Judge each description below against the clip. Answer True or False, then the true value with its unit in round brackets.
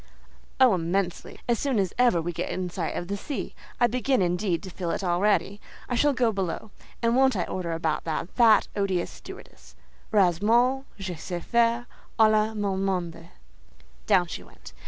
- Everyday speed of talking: True (175 wpm)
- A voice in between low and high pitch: False (195 Hz)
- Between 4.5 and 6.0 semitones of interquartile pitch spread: True (4.9 semitones)